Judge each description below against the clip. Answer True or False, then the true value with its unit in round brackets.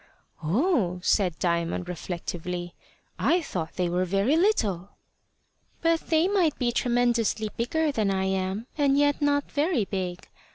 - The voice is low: False (215 Hz)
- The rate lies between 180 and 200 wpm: False (135 wpm)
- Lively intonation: True (8.2 semitones)